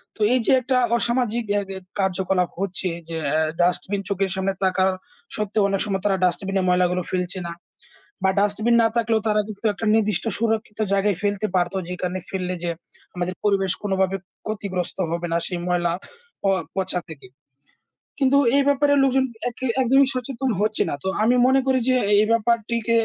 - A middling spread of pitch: Yes, average, 3.8 semitones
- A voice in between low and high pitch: No, high, 200 Hz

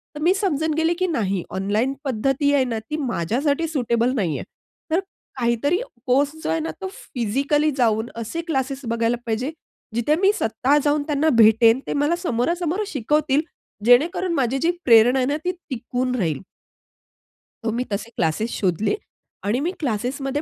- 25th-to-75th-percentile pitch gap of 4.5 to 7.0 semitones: Yes, average, 4.9 semitones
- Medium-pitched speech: No, very high, 260 Hz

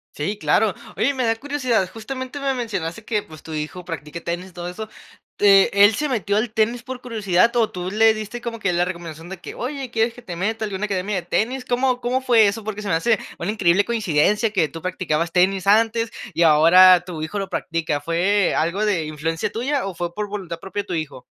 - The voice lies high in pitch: Yes, high, 200 Hz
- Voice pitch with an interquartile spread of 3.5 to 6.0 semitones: Yes, average, 4.7 semitones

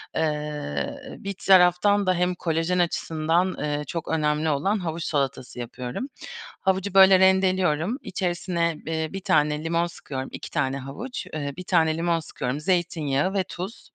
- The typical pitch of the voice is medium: Yes, medium, 165 Hz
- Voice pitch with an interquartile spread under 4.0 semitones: Yes, average, 3.6 semitones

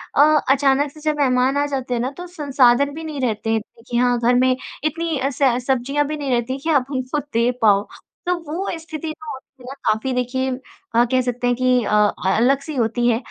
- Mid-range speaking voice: No, very high, 260 Hz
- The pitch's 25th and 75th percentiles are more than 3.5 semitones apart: No, average, 2.9 semitones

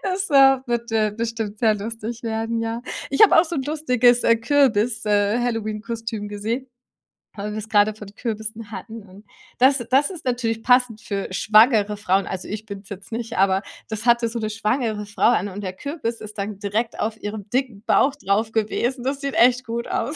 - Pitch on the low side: No, high, 225 Hz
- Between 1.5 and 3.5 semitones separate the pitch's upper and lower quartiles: Yes, average, 2.7 semitones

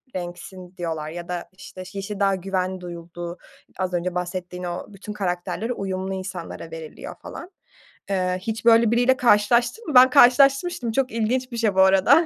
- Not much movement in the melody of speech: No, average, 4.6 semitones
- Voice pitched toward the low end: No, high, 190 Hz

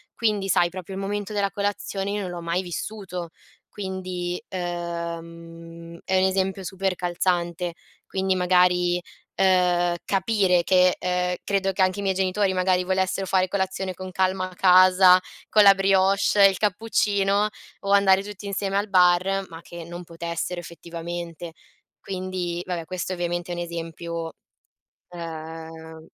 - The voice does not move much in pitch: Yes, narrow, 1.9 semitones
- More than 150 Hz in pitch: Yes, medium, 185 Hz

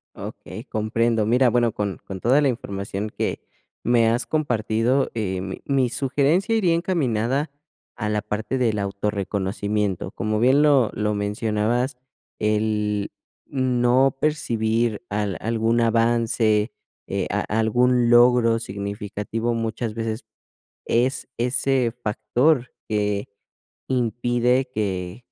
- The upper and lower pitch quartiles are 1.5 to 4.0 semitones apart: Yes, average, 2.9 semitones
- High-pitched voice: No, low, 115 Hz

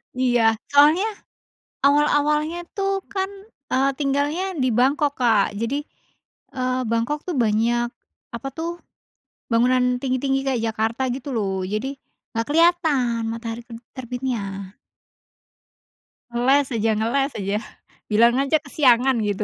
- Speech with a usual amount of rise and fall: Yes, average, 3.8 semitones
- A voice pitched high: Yes, very high, 255 Hz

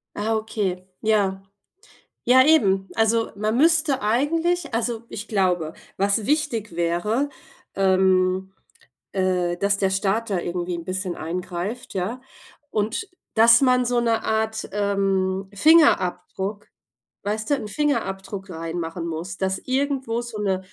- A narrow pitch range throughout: No, average, 3.8 semitones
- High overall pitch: Yes, high, 205 Hz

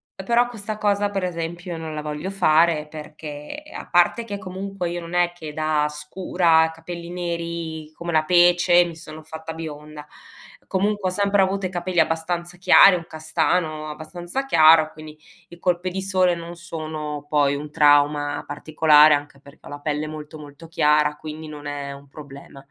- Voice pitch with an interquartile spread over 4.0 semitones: No, average, 2.7 semitones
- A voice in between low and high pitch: Yes, medium, 160 Hz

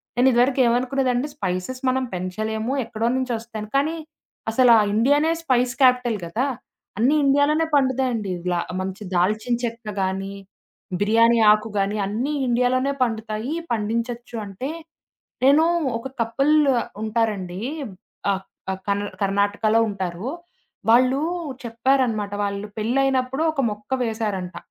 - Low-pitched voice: No, high, 230 Hz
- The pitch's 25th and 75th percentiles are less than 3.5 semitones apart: No, average, 3.8 semitones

